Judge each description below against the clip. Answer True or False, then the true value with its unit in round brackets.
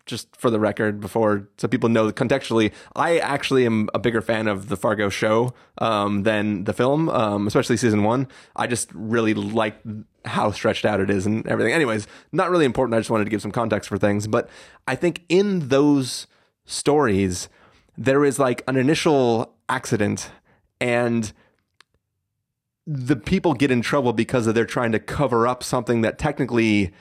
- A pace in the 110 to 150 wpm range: False (180 wpm)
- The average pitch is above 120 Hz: False (115 Hz)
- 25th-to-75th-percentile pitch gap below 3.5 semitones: False (3.8 semitones)